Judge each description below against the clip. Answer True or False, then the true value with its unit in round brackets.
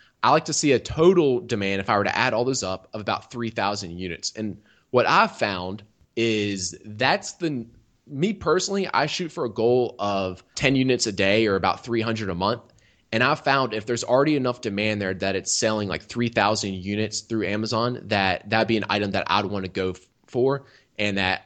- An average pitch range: True (3.8 semitones)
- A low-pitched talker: True (110 Hz)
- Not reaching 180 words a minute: False (205 wpm)